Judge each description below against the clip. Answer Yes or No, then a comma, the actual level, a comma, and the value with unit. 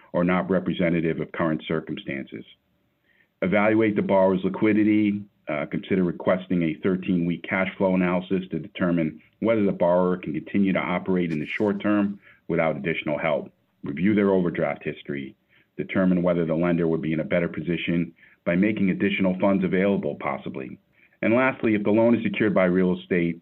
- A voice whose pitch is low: Yes, very low, 95 Hz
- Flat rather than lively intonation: No, average, 3.0 semitones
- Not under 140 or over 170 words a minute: Yes, average, 165 wpm